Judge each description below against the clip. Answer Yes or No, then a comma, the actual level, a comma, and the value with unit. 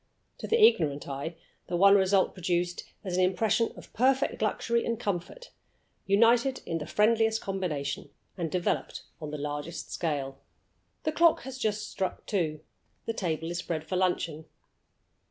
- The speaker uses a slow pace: No, average, 155 wpm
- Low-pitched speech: No, medium, 185 Hz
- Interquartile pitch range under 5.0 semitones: No, wide, 5.6 semitones